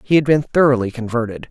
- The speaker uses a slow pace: No, average, 200 wpm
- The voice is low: Yes, low, 130 Hz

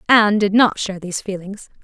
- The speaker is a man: No, female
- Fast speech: No, average, 195 wpm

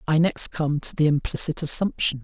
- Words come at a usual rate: Yes, average, 190 wpm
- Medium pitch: Yes, medium, 155 Hz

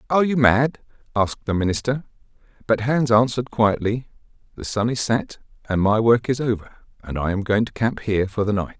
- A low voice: Yes, low, 115 Hz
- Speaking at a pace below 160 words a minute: No, average, 200 wpm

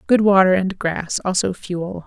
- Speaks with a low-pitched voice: No, medium, 185 Hz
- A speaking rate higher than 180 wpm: No, average, 175 wpm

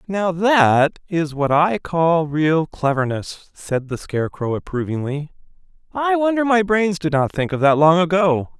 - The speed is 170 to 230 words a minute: No, average, 160 wpm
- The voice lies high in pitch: No, medium, 165 Hz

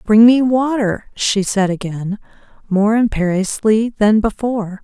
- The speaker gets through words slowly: Yes, slow, 125 wpm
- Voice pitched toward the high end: Yes, high, 210 Hz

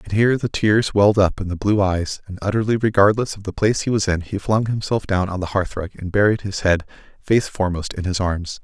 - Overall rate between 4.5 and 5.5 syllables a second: No, 5.9 syllables/s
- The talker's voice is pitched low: Yes, low, 100 Hz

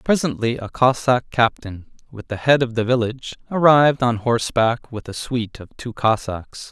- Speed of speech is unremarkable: Yes, average, 170 wpm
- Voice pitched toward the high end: No, low, 120 Hz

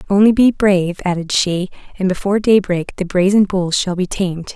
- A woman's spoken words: Yes, female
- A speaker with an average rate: Yes, average, 185 wpm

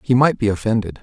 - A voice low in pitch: Yes, low, 115 Hz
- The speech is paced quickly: Yes, fast, 235 wpm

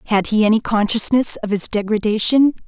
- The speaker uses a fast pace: No, average, 155 wpm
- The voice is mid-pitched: No, high, 220 Hz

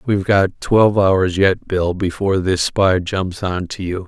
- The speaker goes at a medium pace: Yes, average, 175 wpm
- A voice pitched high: No, very low, 95 Hz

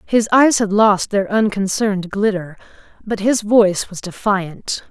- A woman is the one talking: Yes, female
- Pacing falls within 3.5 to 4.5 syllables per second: Yes, 4.2 syllables/s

